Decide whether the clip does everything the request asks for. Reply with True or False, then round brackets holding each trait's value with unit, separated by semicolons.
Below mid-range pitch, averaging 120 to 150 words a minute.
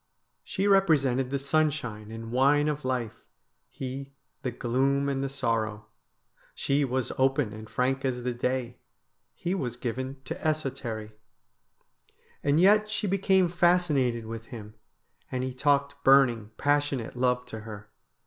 True (130 Hz; 140 wpm)